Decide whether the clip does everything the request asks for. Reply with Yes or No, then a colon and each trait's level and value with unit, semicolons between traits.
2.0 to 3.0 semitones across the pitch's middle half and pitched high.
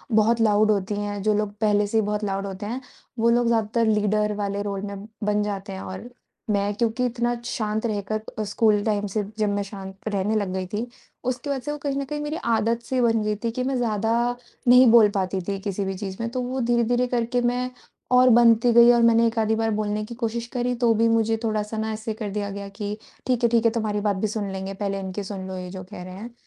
Yes: narrow, 2.5 semitones; high, 215 Hz